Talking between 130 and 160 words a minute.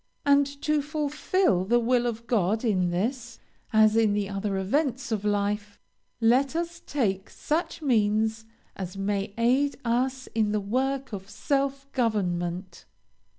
Yes: average, 140 wpm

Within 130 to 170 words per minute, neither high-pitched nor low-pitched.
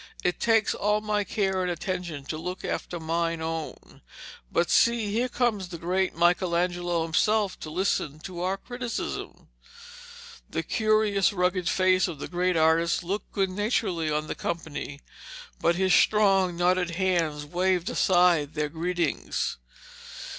Yes: average, 140 wpm; medium, 180 Hz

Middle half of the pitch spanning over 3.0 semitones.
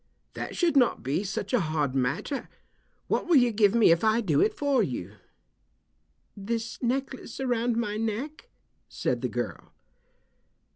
Yes: average, 5.2 semitones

